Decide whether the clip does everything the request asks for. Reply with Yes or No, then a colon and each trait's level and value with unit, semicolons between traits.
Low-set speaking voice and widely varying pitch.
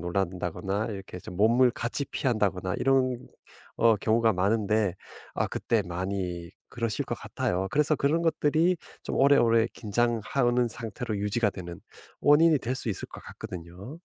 No: low, 110 Hz; average, 4.6 semitones